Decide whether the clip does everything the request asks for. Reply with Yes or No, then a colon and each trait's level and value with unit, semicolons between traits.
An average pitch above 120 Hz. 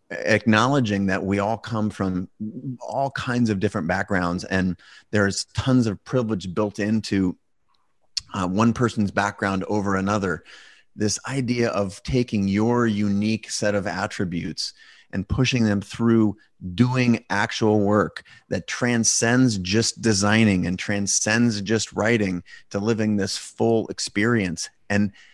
No: low, 105 Hz